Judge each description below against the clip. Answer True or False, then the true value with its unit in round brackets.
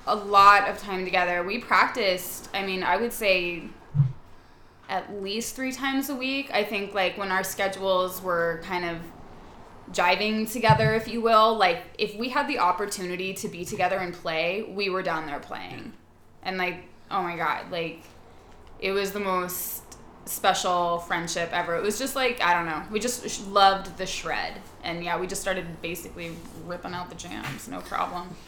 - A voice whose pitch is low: False (185 Hz)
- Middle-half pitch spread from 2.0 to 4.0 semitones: True (2.9 semitones)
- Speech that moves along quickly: False (180 wpm)